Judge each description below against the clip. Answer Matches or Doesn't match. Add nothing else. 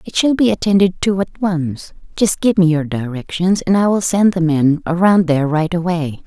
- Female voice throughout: Matches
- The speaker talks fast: Matches